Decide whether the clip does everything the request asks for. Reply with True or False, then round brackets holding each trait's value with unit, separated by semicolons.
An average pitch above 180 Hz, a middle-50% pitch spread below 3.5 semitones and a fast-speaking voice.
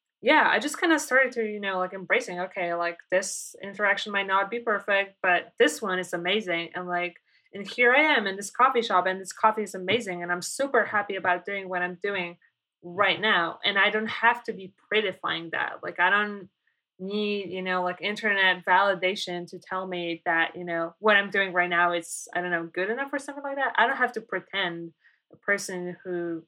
True (190 Hz; 2.9 semitones; 220 wpm)